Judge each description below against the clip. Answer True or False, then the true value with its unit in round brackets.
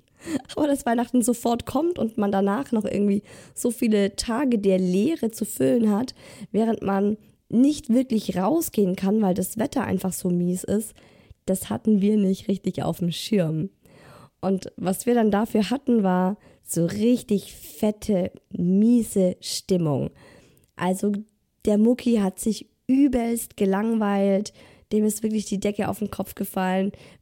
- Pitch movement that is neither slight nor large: True (3.4 semitones)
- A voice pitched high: True (205 Hz)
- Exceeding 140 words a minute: True (150 wpm)